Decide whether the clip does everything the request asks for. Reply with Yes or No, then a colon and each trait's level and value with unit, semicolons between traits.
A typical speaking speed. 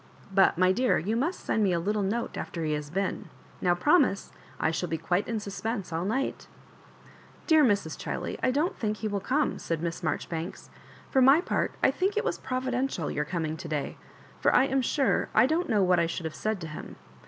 No: fast, 220 wpm